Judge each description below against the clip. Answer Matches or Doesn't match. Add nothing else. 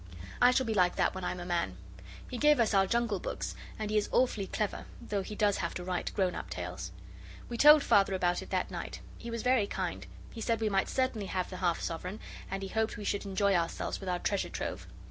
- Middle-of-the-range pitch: Doesn't match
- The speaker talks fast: Matches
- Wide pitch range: Doesn't match